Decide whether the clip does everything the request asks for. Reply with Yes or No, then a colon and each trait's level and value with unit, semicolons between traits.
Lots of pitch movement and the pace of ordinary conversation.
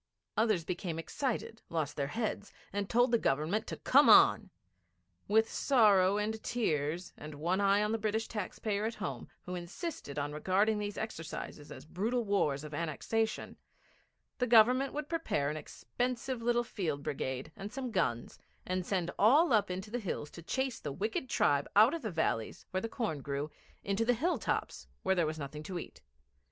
Yes: wide, 6.2 semitones; average, 180 wpm